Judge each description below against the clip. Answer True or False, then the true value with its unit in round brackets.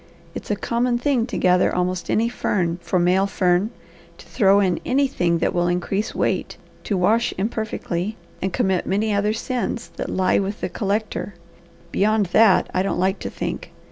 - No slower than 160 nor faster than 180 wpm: True (170 wpm)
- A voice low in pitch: False (200 Hz)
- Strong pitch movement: False (3.3 semitones)